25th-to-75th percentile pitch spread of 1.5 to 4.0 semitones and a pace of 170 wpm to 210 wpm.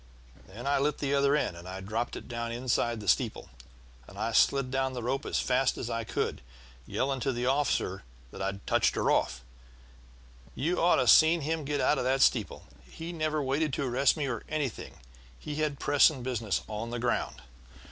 Yes: average, 3.7 semitones; average, 190 wpm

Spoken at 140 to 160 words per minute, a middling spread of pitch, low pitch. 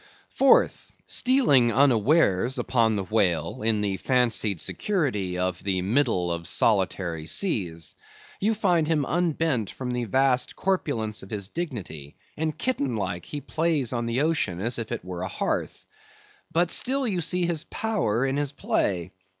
No: average, 155 wpm; wide, 8.7 semitones; low, 120 Hz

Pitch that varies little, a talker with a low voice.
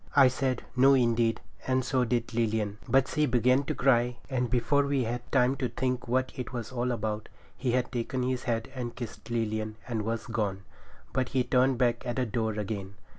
Yes: narrow, 2.1 semitones; low, 120 Hz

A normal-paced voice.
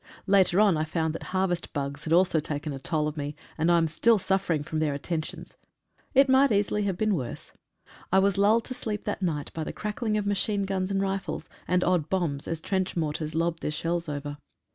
No: fast, 215 wpm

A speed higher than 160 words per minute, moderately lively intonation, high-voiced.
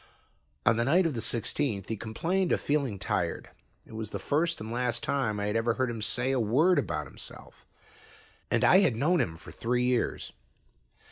No: average, 195 wpm; average, 4.8 semitones; low, 120 Hz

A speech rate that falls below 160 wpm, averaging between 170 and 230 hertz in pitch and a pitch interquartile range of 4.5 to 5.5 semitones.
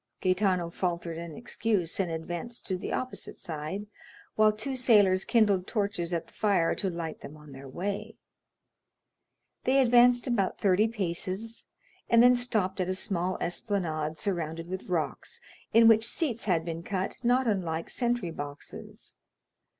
Yes: average, 150 wpm; high, 190 Hz; average, 4.9 semitones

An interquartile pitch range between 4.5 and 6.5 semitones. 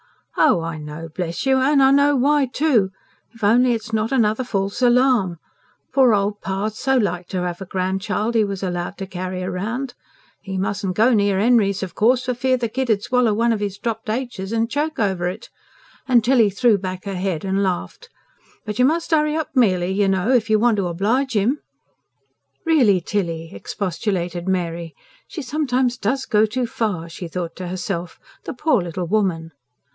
Yes: average, 5.2 semitones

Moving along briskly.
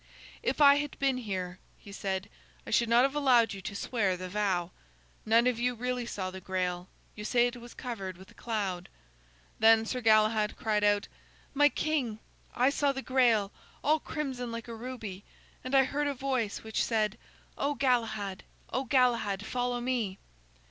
No: average, 175 wpm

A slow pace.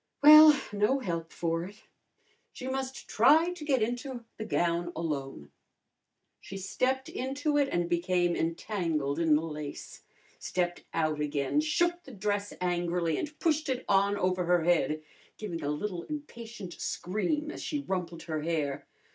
No: average, 150 wpm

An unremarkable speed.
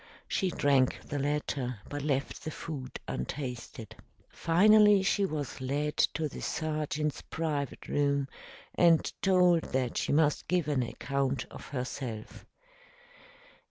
No: slow, 125 wpm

